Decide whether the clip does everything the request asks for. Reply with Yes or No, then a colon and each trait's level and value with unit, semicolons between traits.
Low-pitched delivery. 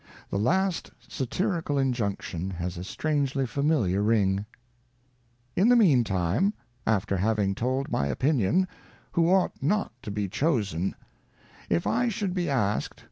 Yes: low, 125 Hz